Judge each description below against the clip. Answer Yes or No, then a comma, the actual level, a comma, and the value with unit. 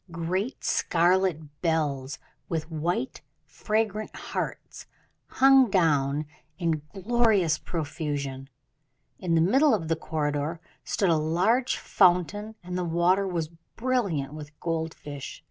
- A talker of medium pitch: Yes, medium, 170 Hz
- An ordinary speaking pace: No, slow, 115 wpm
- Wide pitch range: No, average, 4.1 semitones